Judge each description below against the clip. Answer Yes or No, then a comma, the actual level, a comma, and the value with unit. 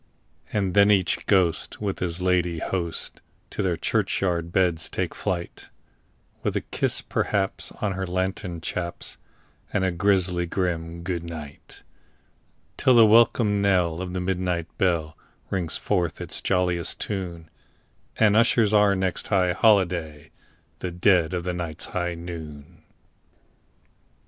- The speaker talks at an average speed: No, slow, 130 wpm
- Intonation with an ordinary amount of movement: No, narrow, 2.3 semitones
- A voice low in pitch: Yes, very low, 90 Hz